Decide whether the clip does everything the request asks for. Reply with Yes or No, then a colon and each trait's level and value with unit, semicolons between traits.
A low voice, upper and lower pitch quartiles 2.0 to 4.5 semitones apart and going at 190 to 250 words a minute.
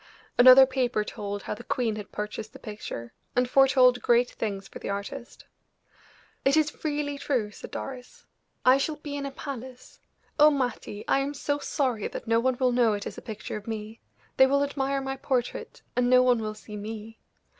No: very high, 250 Hz; average, 4.0 semitones; average, 195 wpm